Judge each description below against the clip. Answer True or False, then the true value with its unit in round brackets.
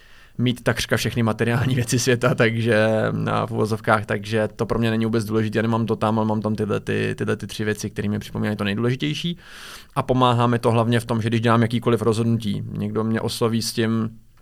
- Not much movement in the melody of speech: True (1.7 semitones)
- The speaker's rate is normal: False (210 wpm)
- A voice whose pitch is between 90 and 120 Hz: True (115 Hz)